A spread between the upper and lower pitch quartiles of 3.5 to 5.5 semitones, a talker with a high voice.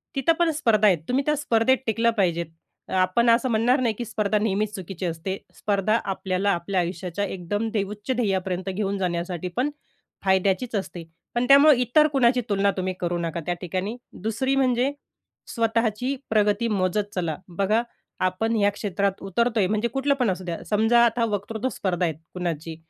Yes: average, 4.0 semitones; high, 205 Hz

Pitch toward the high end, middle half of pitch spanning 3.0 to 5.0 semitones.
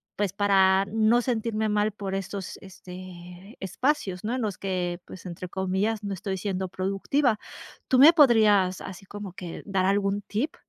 No: high, 195 Hz; narrow, 2.5 semitones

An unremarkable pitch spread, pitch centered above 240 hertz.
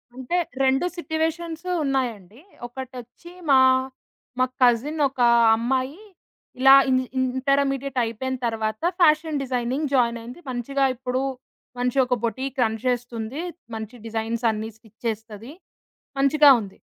Yes: average, 3.1 semitones; very high, 255 Hz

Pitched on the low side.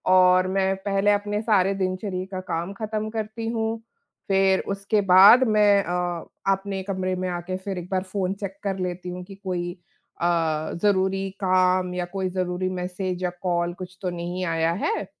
No: medium, 185 Hz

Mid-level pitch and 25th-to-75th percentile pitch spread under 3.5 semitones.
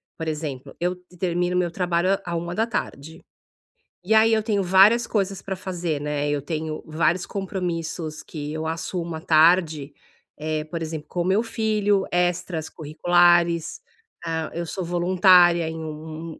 Yes: medium, 170 Hz; average, 2.7 semitones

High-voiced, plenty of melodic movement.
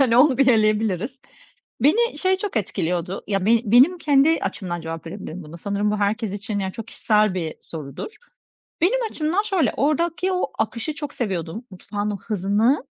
Yes: high, 220 Hz; wide, 7.2 semitones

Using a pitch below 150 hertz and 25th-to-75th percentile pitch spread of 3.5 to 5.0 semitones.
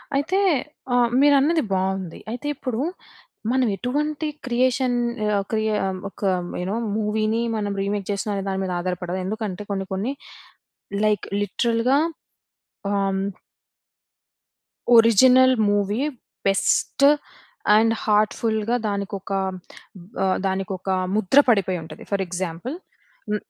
No: high, 210 Hz; average, 4.1 semitones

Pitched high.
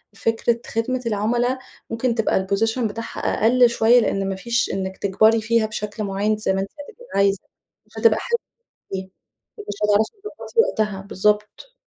Yes: high, 220 Hz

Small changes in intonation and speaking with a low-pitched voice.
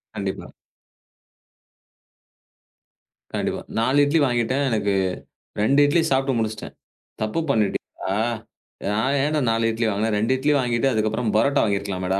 No: average, 4.0 semitones; low, 115 Hz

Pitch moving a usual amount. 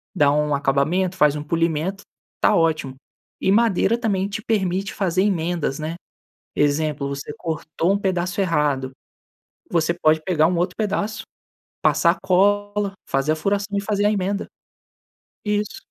Yes: average, 4.5 semitones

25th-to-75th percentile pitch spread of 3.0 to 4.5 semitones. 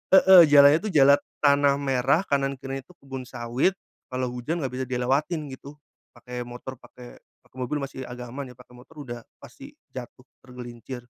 No: narrow, 2.4 semitones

